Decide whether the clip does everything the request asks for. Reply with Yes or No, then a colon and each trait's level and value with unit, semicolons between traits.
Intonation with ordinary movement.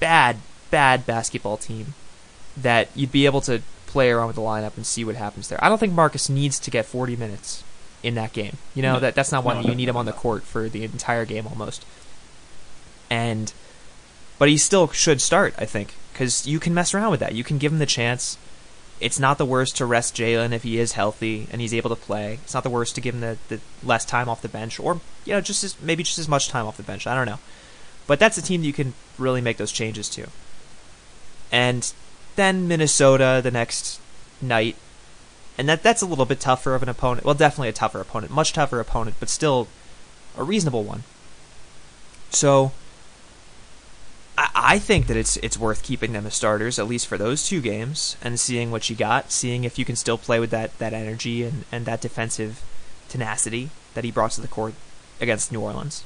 Yes: average, 3.8 semitones